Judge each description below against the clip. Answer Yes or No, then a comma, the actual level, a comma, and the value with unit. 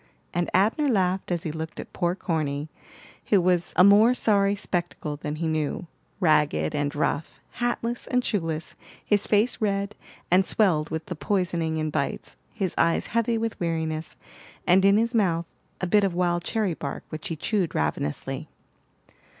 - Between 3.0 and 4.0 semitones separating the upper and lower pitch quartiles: No, average, 4.4 semitones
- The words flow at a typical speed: Yes, average, 165 wpm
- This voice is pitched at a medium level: Yes, medium, 175 Hz